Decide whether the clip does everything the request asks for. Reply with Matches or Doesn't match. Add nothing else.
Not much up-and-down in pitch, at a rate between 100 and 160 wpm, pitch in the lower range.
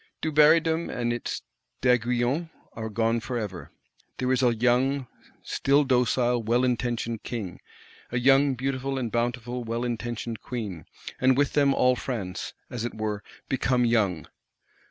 Matches